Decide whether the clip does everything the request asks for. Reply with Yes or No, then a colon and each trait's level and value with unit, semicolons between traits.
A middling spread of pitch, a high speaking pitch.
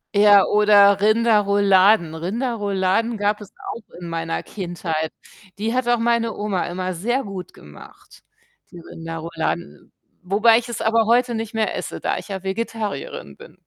Yes: average, 3.7 semitones; high, 205 Hz